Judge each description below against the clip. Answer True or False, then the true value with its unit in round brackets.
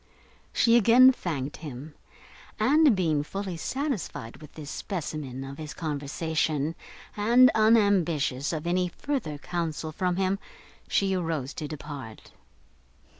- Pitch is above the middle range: False (165 Hz)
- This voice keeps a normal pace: False (120 wpm)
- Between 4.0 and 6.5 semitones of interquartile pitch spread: True (5.3 semitones)